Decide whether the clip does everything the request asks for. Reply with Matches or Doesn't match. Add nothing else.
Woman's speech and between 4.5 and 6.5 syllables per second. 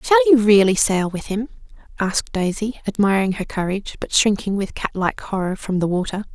Matches